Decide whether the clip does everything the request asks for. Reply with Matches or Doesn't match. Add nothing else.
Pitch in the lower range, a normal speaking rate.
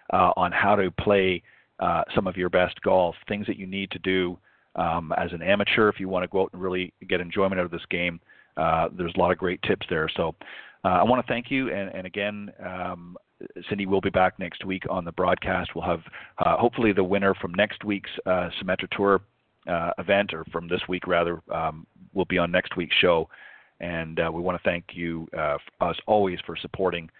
Doesn't match